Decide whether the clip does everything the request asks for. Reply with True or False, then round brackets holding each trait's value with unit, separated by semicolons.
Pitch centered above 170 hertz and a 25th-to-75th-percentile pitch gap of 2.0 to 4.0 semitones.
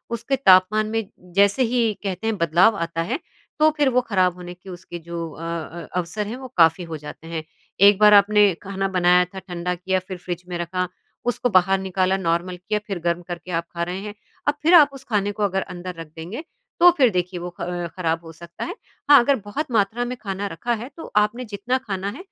True (190 Hz; 3.6 semitones)